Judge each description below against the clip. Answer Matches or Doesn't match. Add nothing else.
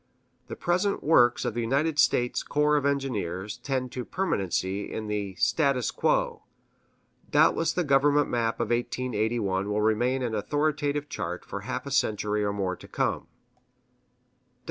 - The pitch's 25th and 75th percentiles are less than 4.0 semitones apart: Doesn't match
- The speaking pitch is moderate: Doesn't match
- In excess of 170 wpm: Doesn't match